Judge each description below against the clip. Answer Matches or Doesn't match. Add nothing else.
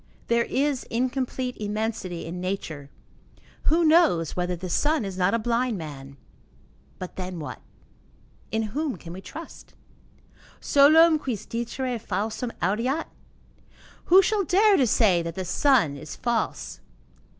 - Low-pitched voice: Doesn't match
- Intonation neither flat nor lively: Doesn't match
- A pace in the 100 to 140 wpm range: Matches